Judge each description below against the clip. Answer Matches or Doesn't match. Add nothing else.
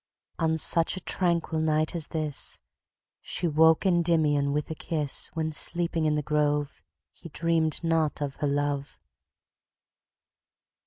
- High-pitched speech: Doesn't match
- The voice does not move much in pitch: Matches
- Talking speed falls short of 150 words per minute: Matches